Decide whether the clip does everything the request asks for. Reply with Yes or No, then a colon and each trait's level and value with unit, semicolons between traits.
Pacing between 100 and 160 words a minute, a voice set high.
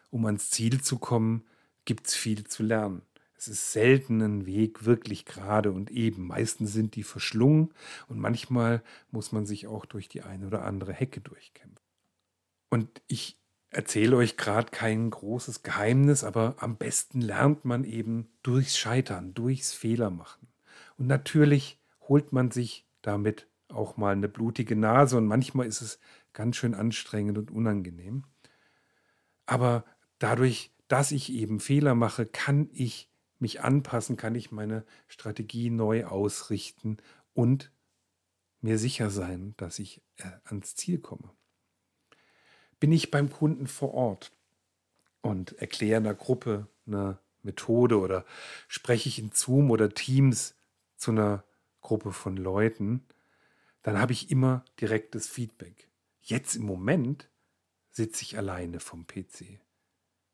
No: average, 140 wpm; low, 115 Hz